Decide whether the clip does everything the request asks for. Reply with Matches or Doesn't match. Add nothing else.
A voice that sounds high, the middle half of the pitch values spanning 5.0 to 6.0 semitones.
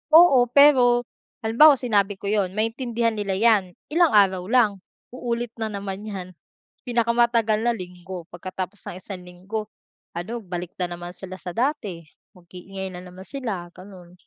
Doesn't match